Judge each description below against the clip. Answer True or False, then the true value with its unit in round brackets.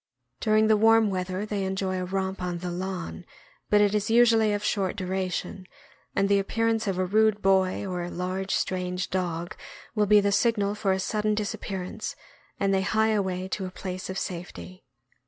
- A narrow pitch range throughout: True (2.3 semitones)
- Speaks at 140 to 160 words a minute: False (190 wpm)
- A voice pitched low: False (195 Hz)